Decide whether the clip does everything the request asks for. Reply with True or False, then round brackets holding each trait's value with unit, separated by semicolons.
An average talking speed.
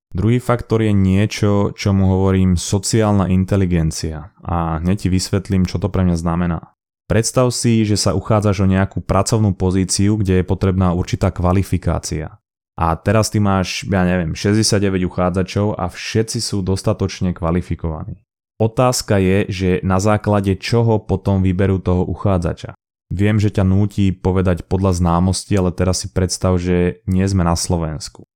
True (150 wpm)